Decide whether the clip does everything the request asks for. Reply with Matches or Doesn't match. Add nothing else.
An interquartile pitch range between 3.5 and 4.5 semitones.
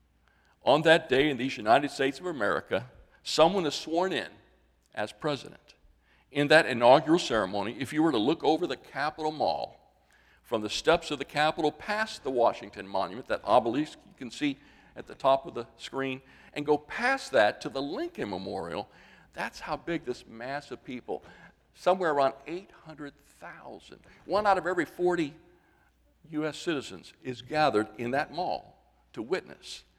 Doesn't match